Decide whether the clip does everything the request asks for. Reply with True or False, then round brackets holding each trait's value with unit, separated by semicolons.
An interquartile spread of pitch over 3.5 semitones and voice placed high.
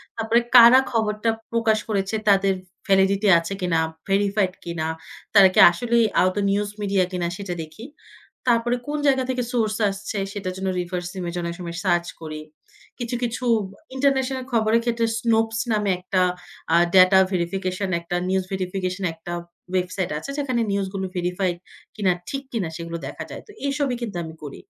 True (4.0 semitones; 195 Hz)